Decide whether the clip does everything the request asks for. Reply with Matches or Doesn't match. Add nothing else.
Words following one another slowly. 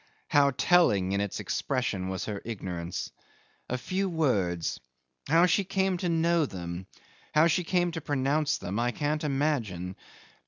Doesn't match